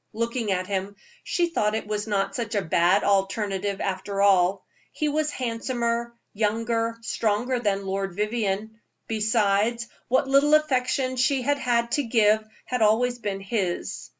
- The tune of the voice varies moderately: Yes, average, 3.5 semitones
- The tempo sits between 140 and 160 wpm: Yes, average, 150 wpm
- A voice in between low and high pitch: No, high, 220 Hz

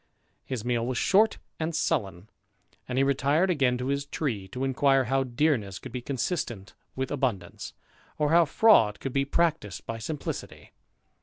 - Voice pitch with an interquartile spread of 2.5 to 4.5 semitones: Yes, average, 4.0 semitones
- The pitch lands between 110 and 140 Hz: Yes, low, 135 Hz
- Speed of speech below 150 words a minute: No, average, 160 wpm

